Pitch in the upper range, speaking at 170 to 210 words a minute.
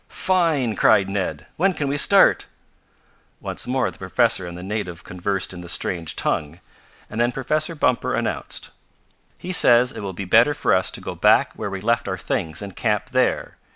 No: low, 105 Hz; average, 190 wpm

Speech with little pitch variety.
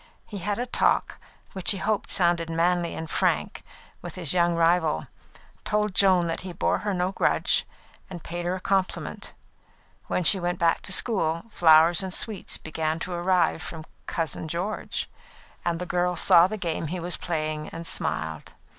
Yes: narrow, 2.2 semitones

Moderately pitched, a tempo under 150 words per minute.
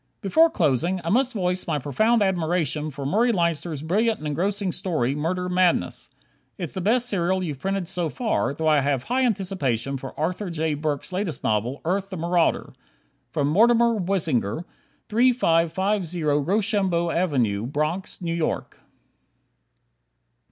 Yes: medium, 175 Hz; slow, 135 wpm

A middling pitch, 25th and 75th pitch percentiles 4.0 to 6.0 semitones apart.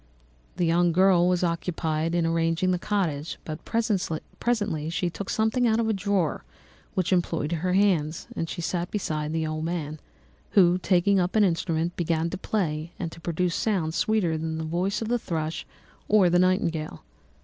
No: medium, 175 Hz; average, 2.9 semitones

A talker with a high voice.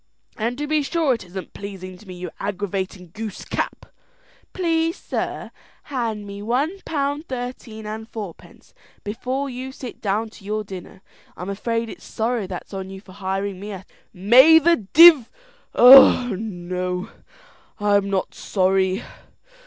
Yes: high, 215 Hz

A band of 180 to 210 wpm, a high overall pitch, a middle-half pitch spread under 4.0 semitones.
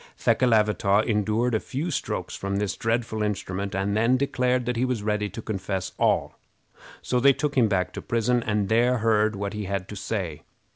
No: average, 190 wpm; low, 110 Hz; average, 3.5 semitones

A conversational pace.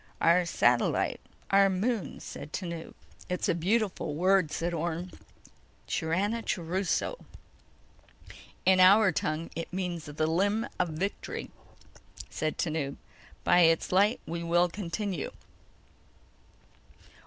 No: slow, 105 wpm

